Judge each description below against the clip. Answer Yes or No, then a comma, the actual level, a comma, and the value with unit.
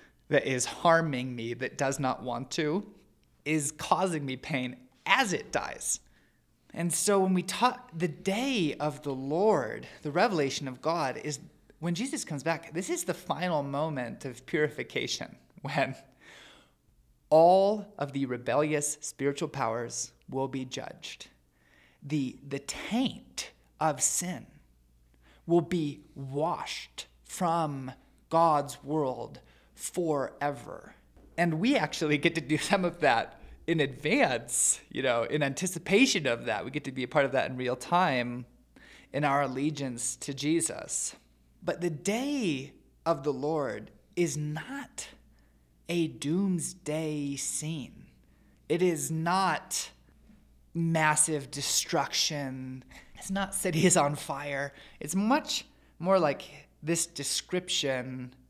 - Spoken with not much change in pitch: No, average, 4.3 semitones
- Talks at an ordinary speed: No, slow, 125 wpm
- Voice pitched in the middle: Yes, medium, 150 Hz